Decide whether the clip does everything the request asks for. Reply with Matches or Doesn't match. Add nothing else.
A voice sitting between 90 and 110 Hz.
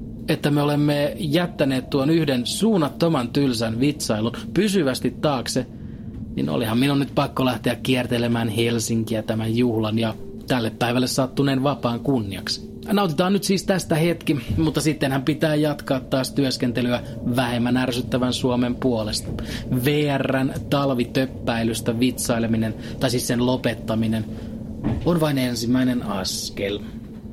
Doesn't match